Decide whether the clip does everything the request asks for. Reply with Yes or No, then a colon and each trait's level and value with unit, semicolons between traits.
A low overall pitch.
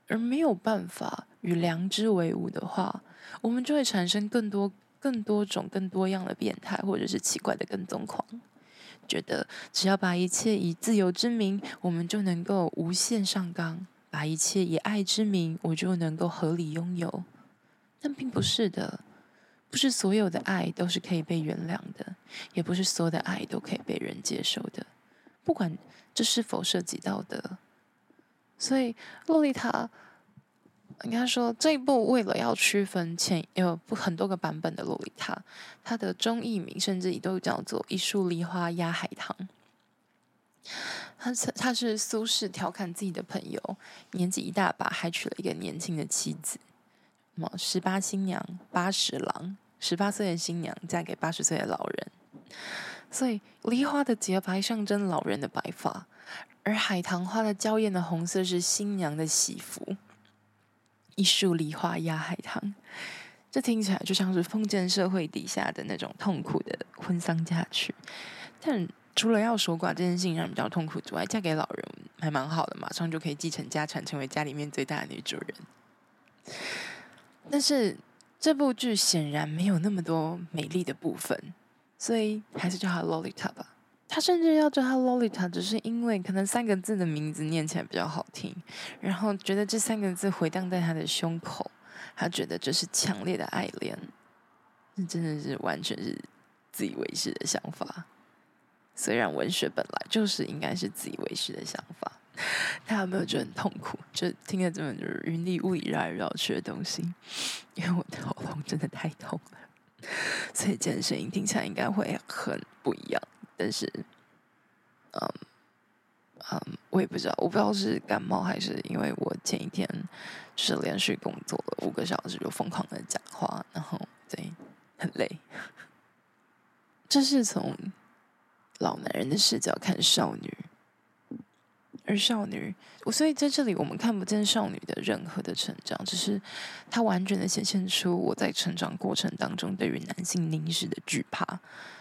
No: high, 190 Hz